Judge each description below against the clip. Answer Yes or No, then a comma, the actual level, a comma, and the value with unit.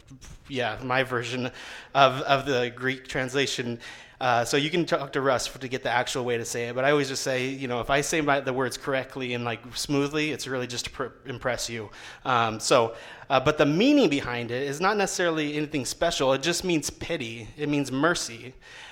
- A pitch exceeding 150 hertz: No, low, 135 Hz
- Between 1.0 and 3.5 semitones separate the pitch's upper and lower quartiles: Yes, average, 3.0 semitones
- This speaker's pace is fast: Yes, fast, 220 wpm